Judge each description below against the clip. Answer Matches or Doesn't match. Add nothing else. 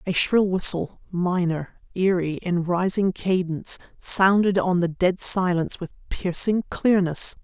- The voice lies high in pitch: Doesn't match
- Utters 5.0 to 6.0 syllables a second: Doesn't match